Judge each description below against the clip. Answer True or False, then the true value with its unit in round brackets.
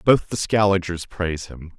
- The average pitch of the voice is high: False (90 Hz)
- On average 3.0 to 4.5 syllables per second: False (4.9 syllables/s)